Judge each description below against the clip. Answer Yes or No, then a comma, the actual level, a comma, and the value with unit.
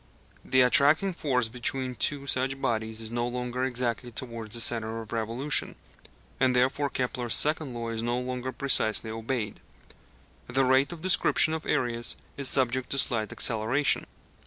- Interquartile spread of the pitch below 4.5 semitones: Yes, narrow, 2.5 semitones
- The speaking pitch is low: Yes, low, 125 Hz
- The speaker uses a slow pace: No, average, 155 wpm